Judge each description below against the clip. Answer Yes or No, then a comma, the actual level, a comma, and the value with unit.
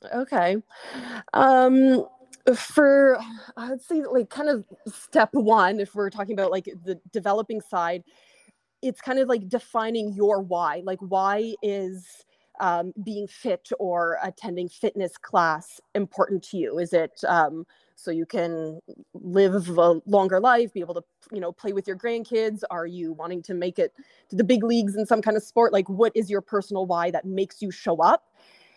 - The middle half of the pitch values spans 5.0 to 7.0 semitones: No, average, 4.2 semitones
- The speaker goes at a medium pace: Yes, average, 175 wpm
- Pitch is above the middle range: Yes, high, 200 Hz